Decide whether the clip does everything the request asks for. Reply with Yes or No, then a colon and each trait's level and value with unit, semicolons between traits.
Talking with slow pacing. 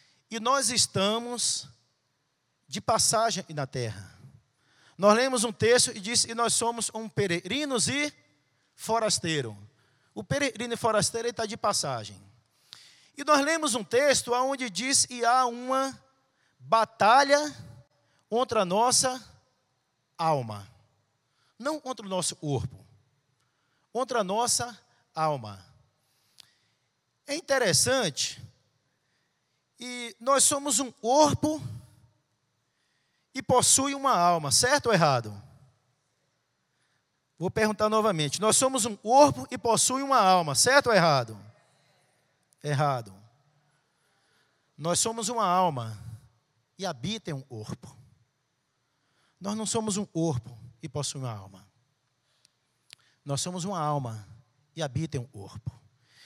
Yes: slow, 110 wpm